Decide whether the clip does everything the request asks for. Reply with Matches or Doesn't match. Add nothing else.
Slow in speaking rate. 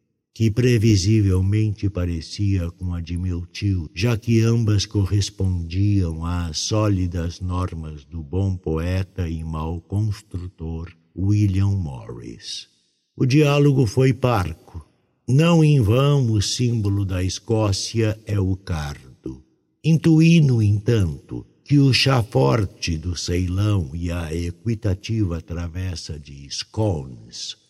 Matches